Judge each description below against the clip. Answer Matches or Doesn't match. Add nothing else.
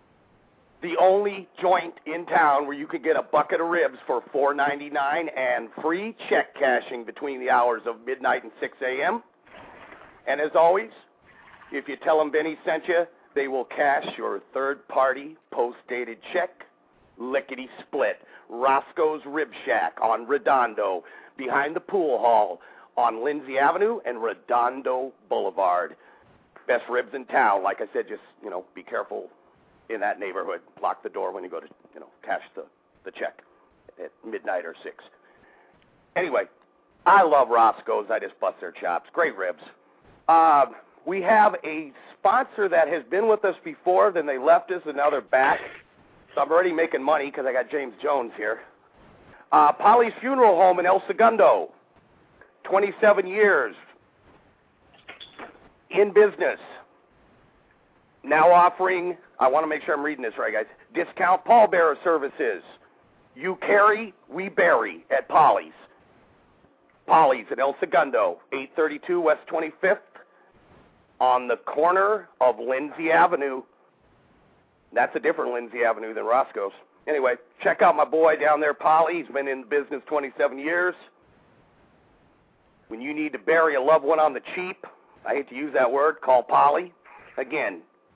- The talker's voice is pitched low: Doesn't match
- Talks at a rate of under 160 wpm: Matches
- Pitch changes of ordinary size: Doesn't match